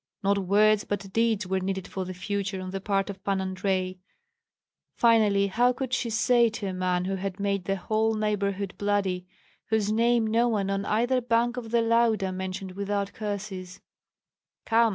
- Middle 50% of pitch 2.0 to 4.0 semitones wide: Yes, average, 2.7 semitones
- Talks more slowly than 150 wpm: No, average, 175 wpm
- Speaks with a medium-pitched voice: No, high, 200 Hz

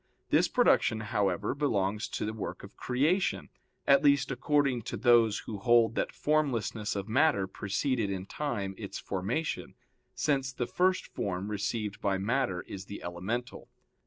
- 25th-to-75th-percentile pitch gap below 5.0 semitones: No, wide, 5.4 semitones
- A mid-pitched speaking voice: No, low, 110 Hz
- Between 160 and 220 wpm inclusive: No, average, 150 wpm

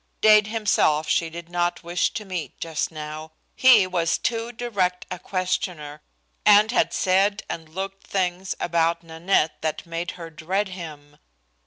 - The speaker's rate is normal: Yes, average, 150 wpm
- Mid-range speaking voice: Yes, medium, 175 Hz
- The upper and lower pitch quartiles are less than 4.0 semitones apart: Yes, average, 3.2 semitones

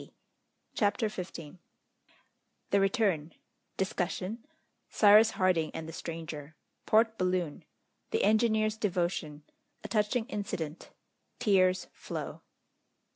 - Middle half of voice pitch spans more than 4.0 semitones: Yes, average, 4.5 semitones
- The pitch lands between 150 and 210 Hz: Yes, high, 190 Hz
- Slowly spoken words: Yes, slow, 95 wpm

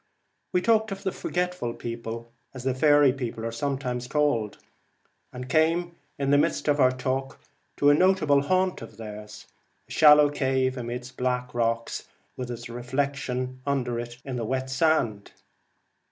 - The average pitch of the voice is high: No, low, 130 Hz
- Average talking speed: Yes, average, 160 wpm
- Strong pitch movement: No, average, 3.4 semitones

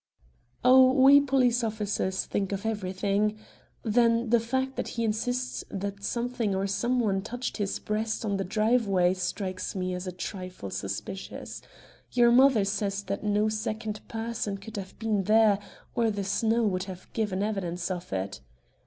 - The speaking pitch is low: No, high, 210 Hz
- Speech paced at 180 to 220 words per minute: No, average, 160 wpm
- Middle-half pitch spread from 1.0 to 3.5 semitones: Yes, average, 3.2 semitones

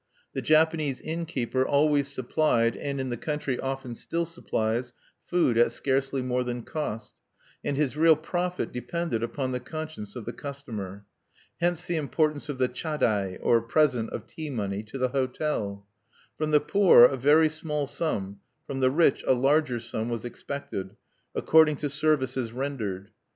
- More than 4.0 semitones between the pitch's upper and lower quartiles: Yes, average, 4.4 semitones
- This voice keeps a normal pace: Yes, average, 160 wpm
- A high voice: No, low, 135 Hz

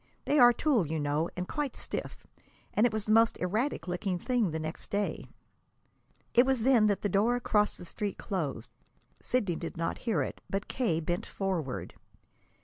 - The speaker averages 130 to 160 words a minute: No, average, 180 wpm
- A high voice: Yes, high, 205 Hz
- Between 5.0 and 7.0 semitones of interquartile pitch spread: Yes, wide, 5.4 semitones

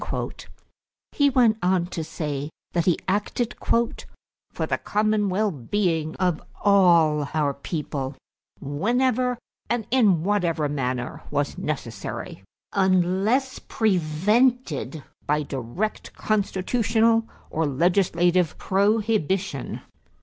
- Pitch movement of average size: No, wide, 6.0 semitones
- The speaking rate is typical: No, slow, 95 wpm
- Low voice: No, medium, 185 Hz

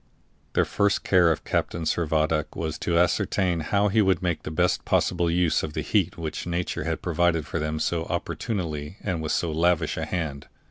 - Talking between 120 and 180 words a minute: No, average, 190 wpm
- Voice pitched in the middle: No, very low, 85 Hz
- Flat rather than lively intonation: Yes, narrow, 2.3 semitones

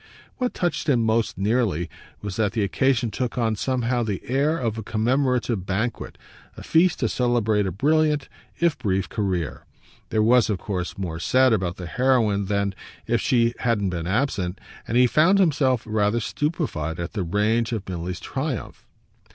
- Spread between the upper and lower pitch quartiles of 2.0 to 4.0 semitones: No, average, 4.6 semitones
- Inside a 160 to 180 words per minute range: Yes, average, 165 wpm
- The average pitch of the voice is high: No, low, 115 Hz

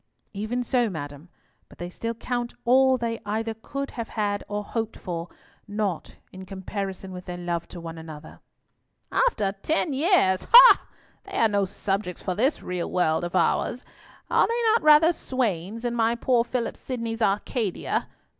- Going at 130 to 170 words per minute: Yes, average, 165 wpm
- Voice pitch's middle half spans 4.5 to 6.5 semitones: Yes, average, 5.0 semitones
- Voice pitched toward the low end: No, high, 215 Hz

